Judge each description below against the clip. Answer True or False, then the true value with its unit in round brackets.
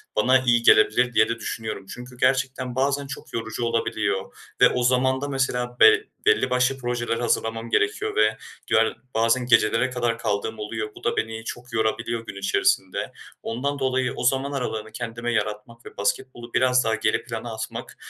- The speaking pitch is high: False (120 Hz)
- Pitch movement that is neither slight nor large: False (2.3 semitones)